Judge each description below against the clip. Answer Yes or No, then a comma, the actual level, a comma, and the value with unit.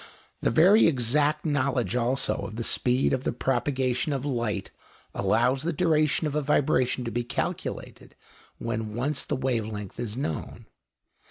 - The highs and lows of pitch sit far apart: No, average, 3.6 semitones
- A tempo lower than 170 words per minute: Yes, average, 155 wpm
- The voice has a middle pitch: No, low, 130 Hz